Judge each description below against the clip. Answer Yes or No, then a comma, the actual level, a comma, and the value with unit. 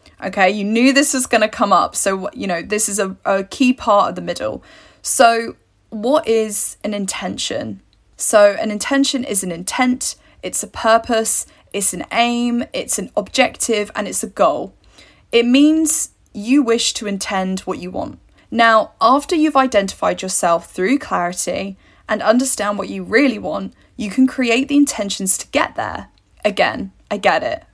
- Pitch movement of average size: Yes, average, 4.8 semitones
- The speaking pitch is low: No, high, 220 Hz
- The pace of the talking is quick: No, average, 170 wpm